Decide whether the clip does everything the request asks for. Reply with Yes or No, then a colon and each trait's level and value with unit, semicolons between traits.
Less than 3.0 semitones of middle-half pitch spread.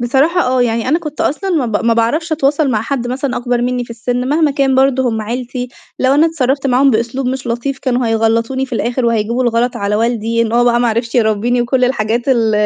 Yes: narrow, 2.5 semitones